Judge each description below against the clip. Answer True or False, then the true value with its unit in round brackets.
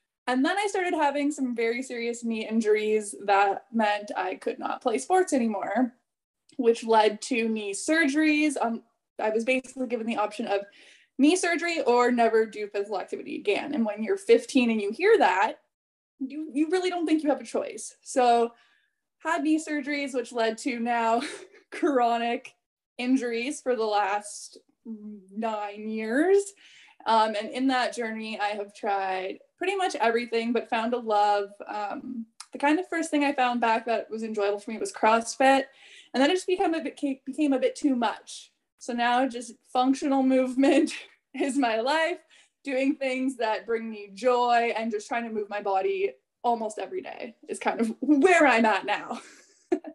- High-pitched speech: True (245 Hz)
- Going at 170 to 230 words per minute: True (175 wpm)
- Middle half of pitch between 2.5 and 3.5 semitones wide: False (5.0 semitones)